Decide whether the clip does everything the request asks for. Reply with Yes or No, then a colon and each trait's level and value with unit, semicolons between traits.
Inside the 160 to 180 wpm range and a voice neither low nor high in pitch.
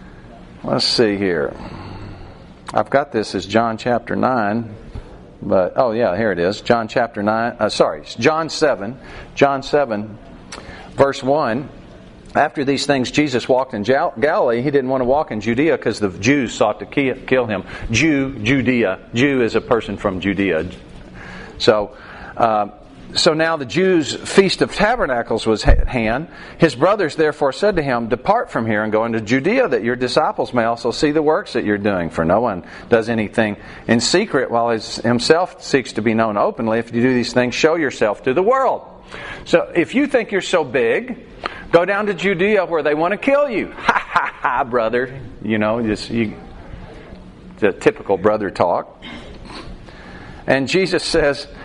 No: average, 175 wpm; low, 120 Hz